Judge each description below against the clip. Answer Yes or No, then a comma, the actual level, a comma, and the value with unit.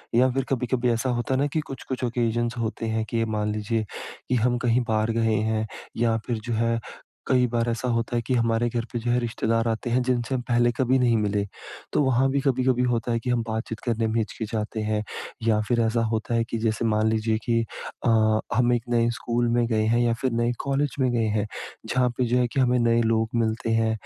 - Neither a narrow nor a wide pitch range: No, narrow, 1.6 semitones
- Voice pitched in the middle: No, low, 115 Hz